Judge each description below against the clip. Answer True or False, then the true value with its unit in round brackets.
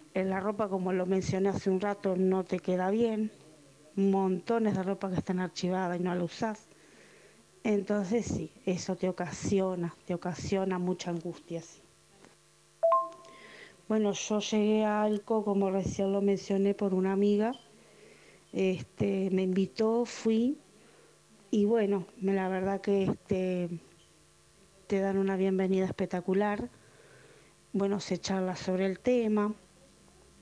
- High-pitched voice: True (195 Hz)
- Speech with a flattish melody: True (2.0 semitones)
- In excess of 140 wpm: False (130 wpm)